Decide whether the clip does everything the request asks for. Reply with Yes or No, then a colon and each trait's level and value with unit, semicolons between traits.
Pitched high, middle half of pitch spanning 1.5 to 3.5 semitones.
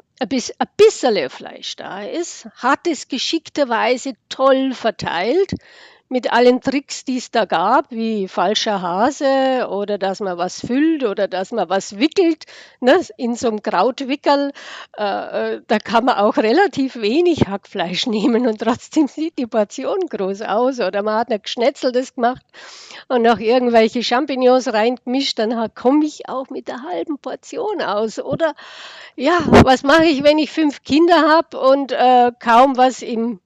No: very high, 255 Hz; average, 4.5 semitones